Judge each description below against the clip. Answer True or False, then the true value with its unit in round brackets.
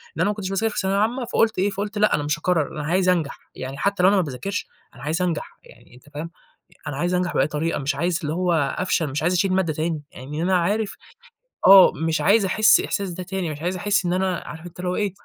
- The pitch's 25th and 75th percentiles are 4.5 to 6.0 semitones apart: False (3.7 semitones)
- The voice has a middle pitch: True (180 Hz)